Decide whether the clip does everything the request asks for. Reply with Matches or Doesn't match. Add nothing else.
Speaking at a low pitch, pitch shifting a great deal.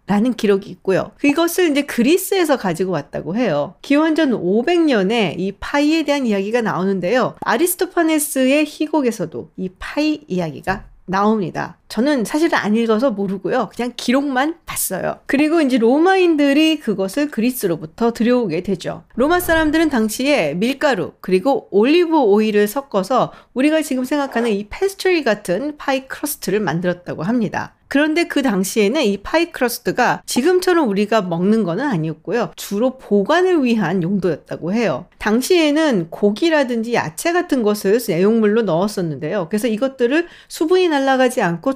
Doesn't match